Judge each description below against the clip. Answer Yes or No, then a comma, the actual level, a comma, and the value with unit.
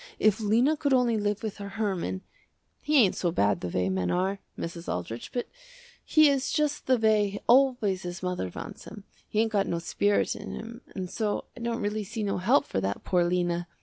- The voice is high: Yes, high, 205 Hz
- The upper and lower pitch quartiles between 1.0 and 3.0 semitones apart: No, average, 4.6 semitones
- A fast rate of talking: Yes, fast, 210 wpm